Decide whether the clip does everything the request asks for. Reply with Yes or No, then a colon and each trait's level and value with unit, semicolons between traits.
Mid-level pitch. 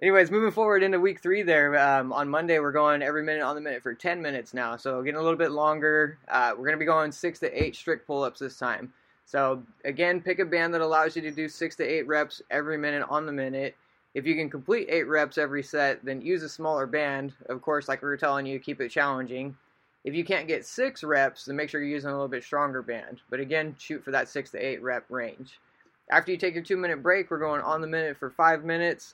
Yes: medium, 150 Hz